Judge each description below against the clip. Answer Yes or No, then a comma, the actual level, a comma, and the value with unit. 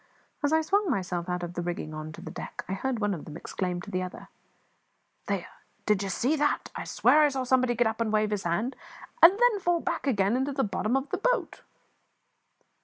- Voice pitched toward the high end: Yes, high, 225 Hz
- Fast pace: Yes, fast, 225 wpm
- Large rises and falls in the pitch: Yes, wide, 7.8 semitones